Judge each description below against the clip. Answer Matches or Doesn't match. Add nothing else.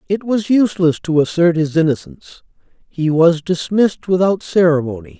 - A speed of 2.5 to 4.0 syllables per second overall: Doesn't match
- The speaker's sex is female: Doesn't match